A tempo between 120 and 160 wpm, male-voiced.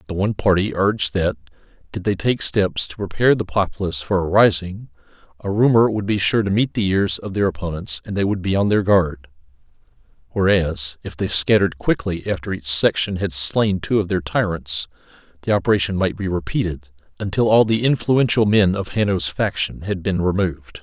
No: average, 185 wpm; male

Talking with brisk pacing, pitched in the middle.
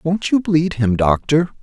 No: average, 185 wpm; medium, 155 Hz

